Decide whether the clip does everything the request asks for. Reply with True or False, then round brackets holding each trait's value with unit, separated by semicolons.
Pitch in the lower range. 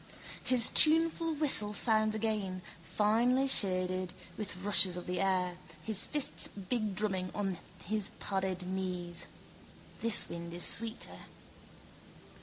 False (200 Hz)